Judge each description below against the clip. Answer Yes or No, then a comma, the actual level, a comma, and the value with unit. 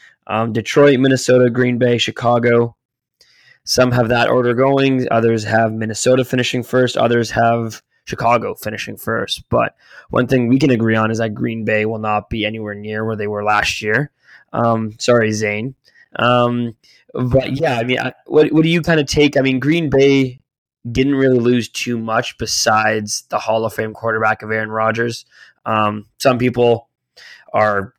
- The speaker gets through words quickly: No, average, 170 wpm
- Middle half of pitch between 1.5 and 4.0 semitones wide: Yes, average, 2.7 semitones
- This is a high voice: No, low, 120 Hz